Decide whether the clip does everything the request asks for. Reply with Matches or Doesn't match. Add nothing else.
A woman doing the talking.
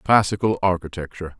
Doesn't match